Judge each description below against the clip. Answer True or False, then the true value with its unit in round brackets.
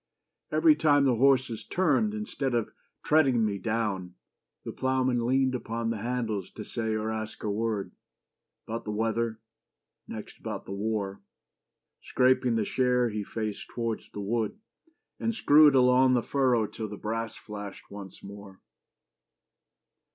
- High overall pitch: False (115 Hz)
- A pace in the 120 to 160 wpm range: True (145 wpm)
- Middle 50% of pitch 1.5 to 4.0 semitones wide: True (3.3 semitones)